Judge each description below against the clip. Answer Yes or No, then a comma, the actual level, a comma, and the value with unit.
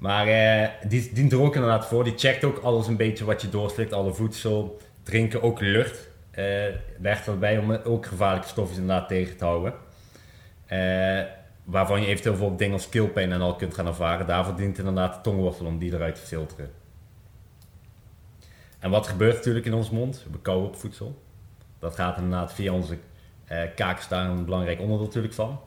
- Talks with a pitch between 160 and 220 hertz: No, low, 100 Hz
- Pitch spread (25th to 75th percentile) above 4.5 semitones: No, average, 3.3 semitones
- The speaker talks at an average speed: Yes, average, 185 wpm